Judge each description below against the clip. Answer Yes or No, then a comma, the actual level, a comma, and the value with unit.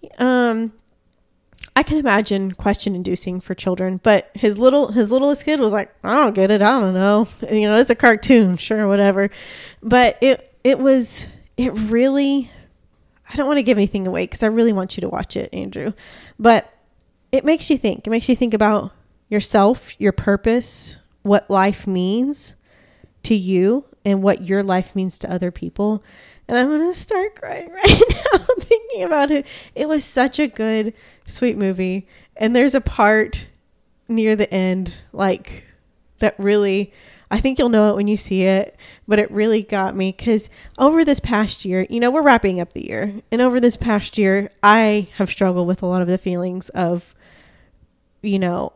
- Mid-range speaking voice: No, high, 215 Hz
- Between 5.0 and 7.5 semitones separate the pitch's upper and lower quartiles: No, average, 4.3 semitones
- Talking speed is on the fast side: No, average, 185 wpm